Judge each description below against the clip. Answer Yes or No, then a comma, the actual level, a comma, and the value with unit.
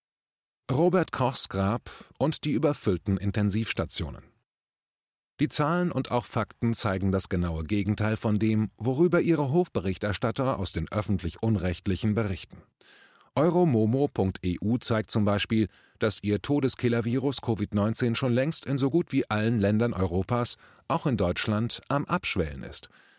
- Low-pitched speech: Yes, low, 115 Hz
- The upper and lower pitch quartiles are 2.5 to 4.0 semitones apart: No, average, 4.8 semitones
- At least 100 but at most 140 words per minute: Yes, slow, 125 wpm